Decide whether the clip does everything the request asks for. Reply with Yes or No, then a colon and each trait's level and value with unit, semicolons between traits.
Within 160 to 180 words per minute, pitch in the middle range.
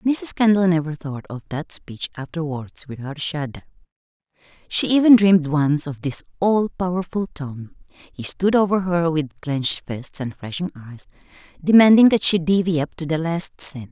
Yes: average, 165 wpm; medium, 165 Hz